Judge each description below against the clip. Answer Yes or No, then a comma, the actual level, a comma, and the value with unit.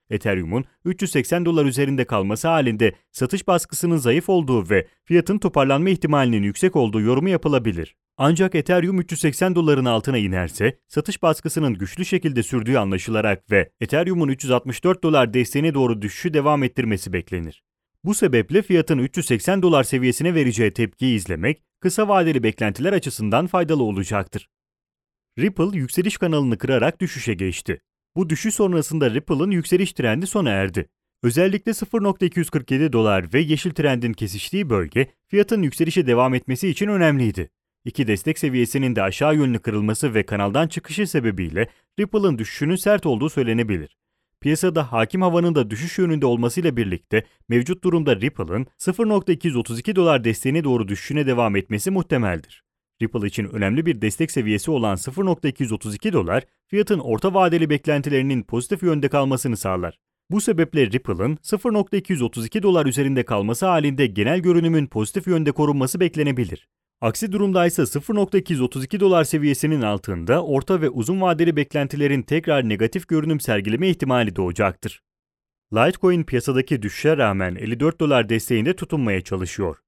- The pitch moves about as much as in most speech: No, wide, 7.1 semitones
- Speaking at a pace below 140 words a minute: Yes, average, 130 wpm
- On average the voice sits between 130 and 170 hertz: Yes, medium, 140 Hz